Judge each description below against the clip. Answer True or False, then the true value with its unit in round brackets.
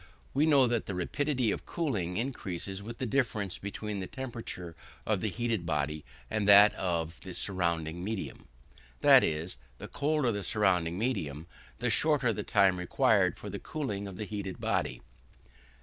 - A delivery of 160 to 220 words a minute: True (165 wpm)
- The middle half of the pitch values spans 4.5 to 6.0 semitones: True (4.9 semitones)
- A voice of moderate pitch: False (100 Hz)